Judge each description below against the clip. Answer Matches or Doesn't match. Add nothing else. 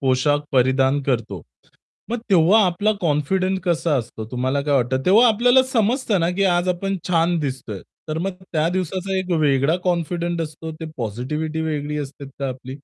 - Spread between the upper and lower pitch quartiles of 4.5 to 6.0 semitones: Matches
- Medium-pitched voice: Matches